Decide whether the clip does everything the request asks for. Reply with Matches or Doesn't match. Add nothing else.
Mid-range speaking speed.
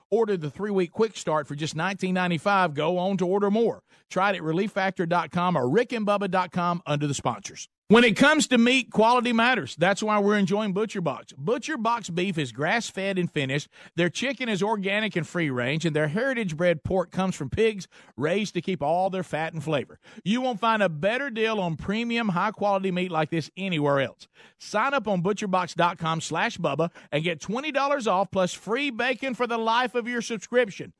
Matches